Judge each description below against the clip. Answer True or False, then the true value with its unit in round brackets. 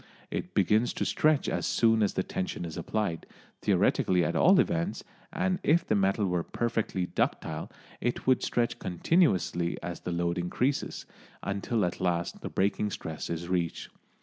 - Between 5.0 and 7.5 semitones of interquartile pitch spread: True (5.4 semitones)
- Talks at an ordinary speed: True (160 wpm)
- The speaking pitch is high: False (95 Hz)